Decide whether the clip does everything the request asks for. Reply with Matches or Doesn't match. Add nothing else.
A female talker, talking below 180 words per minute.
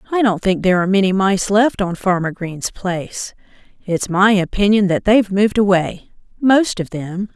Matches